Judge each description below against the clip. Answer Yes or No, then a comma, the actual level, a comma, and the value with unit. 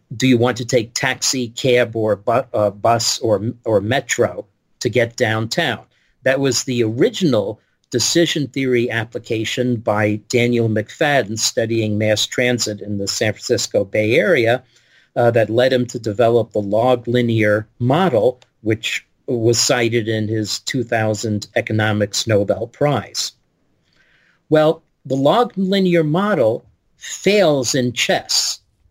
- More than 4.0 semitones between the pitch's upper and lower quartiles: No, average, 2.8 semitones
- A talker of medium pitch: No, low, 120 Hz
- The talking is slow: Yes, slow, 130 wpm